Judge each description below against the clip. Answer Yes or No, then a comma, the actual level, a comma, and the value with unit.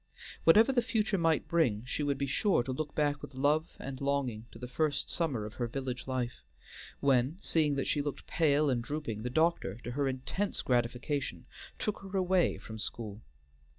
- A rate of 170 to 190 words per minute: Yes, average, 185 wpm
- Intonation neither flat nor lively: Yes, average, 4.6 semitones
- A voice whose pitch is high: No, medium, 140 Hz